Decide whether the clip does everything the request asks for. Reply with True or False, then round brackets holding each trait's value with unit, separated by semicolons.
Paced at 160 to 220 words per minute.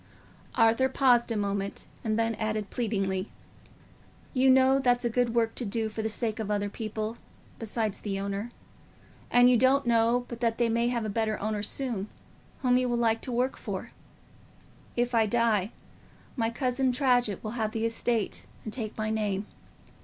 True (175 wpm)